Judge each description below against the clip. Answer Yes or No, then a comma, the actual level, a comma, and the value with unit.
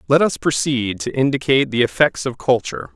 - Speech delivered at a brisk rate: No, average, 185 wpm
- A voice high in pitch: No, low, 130 Hz